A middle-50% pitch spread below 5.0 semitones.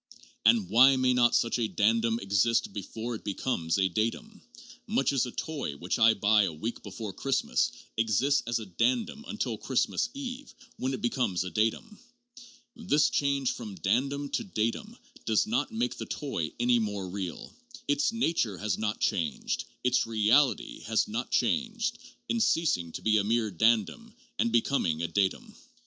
No: wide, 5.5 semitones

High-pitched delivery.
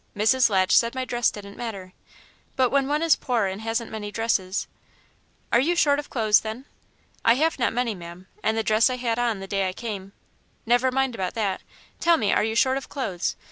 Yes: high, 230 Hz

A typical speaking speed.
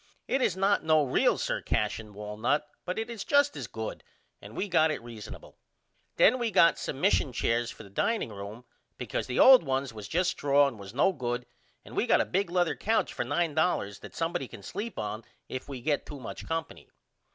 No: fast, 210 wpm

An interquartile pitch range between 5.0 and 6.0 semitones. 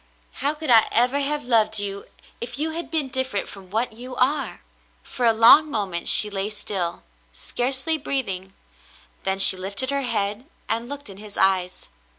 Yes: average, 5.3 semitones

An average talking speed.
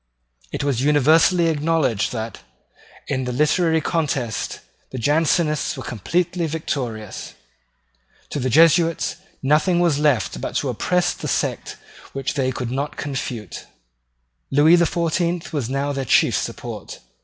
No: slow, 130 wpm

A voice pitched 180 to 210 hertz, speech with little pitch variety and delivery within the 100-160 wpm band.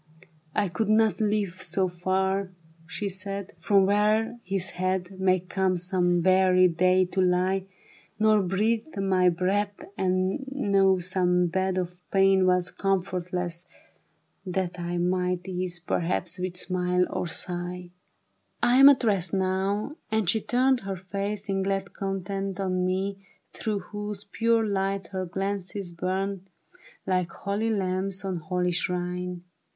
Yes: high, 190 Hz; narrow, 1.6 semitones; average, 140 wpm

